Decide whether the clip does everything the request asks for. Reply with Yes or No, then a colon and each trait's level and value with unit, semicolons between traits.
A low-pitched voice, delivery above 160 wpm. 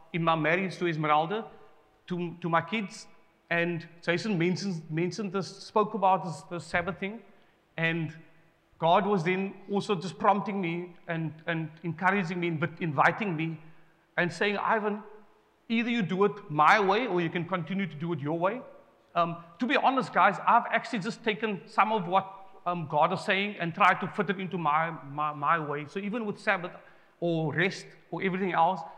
No: medium, 180 Hz; average, 180 wpm